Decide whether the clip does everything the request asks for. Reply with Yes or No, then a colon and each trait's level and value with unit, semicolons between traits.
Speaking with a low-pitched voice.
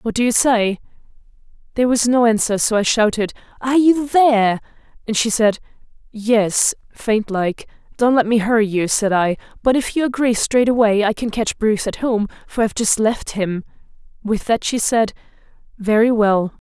No: high, 225 Hz